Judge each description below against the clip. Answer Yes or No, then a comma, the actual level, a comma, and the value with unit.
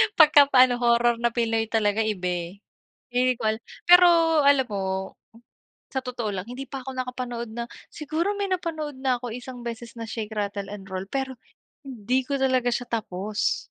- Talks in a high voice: Yes, high, 245 Hz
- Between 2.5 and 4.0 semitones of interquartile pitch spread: Yes, average, 3.3 semitones